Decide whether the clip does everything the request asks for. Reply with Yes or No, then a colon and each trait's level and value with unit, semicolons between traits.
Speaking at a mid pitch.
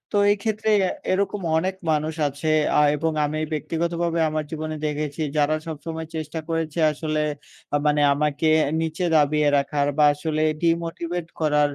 Yes: medium, 155 Hz